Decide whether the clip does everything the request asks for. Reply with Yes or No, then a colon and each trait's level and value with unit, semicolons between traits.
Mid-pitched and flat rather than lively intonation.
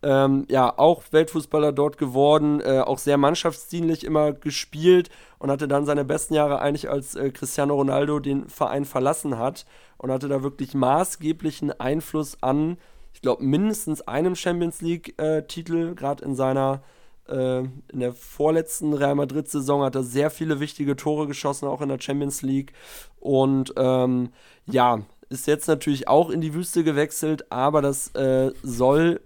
Yes: medium, 145 Hz; narrow, 2.3 semitones